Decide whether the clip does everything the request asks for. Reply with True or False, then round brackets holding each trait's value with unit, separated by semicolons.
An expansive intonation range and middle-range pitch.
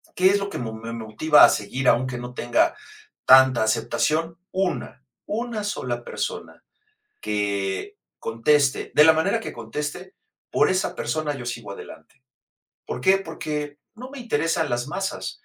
True (7.3 semitones; 145 Hz)